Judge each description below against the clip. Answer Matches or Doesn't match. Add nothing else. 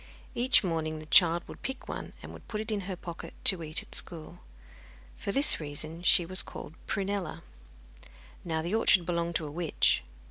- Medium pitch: Matches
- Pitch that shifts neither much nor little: Matches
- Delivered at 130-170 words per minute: Doesn't match